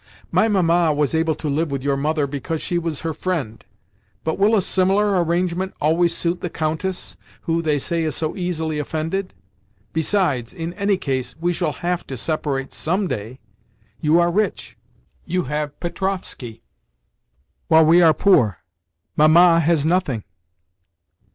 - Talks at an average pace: Yes, average, 145 wpm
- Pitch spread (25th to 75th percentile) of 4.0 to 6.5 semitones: No, average, 3.4 semitones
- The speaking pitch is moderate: Yes, medium, 160 Hz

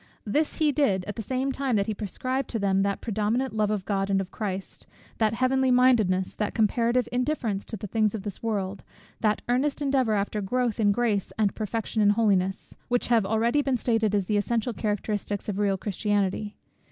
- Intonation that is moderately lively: Yes, average, 3.3 semitones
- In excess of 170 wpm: Yes, average, 195 wpm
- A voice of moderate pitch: No, high, 215 Hz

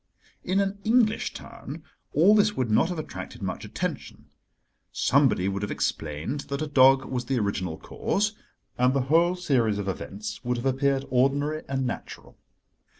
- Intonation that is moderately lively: No, wide, 6.0 semitones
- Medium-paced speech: Yes, average, 160 wpm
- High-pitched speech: No, low, 135 Hz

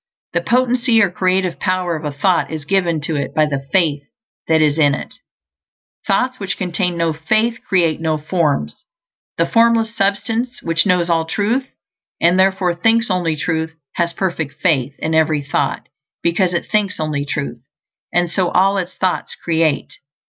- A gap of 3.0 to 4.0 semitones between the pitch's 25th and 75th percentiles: Yes, average, 3.7 semitones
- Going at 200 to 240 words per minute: No, average, 165 wpm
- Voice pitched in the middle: Yes, medium, 175 Hz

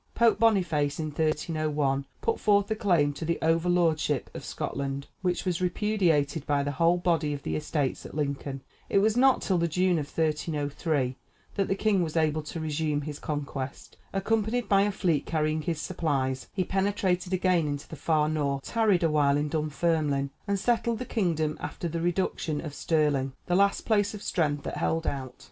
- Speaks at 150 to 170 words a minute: No, average, 185 wpm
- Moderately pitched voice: Yes, medium, 160 Hz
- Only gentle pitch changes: No, average, 4.2 semitones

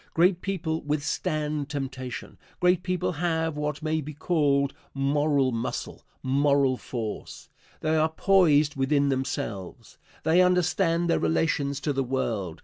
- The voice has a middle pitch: Yes, medium, 150 Hz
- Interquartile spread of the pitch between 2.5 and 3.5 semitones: Yes, average, 2.9 semitones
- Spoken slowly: Yes, slow, 130 wpm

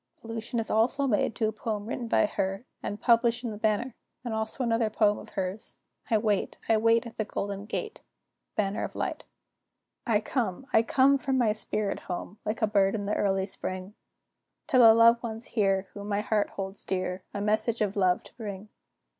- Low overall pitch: No, high, 215 Hz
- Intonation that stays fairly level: Yes, narrow, 2.2 semitones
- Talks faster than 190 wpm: Yes, average, 200 wpm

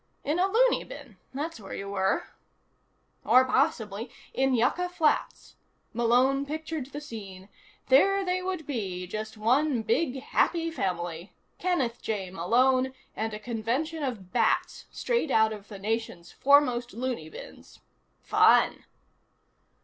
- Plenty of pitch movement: Yes, wide, 5.7 semitones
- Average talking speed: No, slow, 130 wpm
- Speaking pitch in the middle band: No, very high, 250 Hz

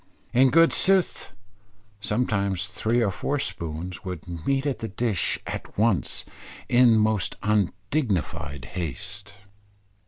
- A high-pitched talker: No, low, 105 Hz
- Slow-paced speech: Yes, slow, 115 wpm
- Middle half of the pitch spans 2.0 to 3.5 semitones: No, average, 5.0 semitones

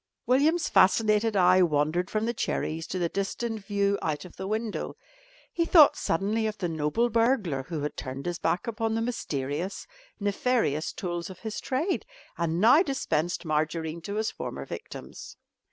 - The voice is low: No, high, 195 Hz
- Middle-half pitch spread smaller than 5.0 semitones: No, wide, 5.6 semitones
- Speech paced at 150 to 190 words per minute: Yes, average, 165 wpm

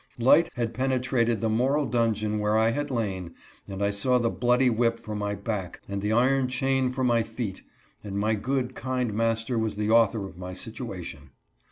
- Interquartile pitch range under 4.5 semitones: Yes, average, 3.2 semitones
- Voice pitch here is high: No, low, 115 Hz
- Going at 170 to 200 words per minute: Yes, average, 185 wpm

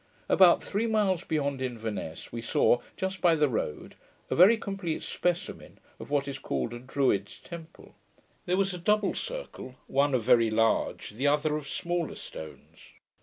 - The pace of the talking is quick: No, average, 165 wpm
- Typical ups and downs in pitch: No, wide, 6.9 semitones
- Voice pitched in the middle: Yes, medium, 150 Hz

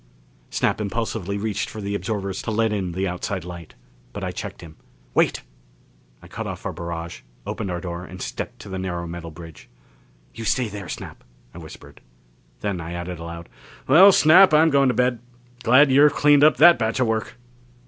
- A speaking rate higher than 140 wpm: Yes, average, 190 wpm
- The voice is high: No, low, 100 Hz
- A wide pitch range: Yes, wide, 6.2 semitones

